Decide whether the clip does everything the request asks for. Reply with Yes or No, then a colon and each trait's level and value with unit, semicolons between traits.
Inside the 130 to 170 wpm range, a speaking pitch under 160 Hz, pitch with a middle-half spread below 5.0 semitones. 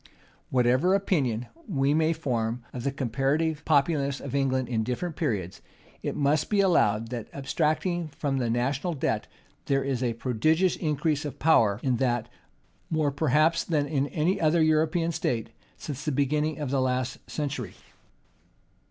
Yes: average, 150 wpm; medium, 140 Hz; average, 3.8 semitones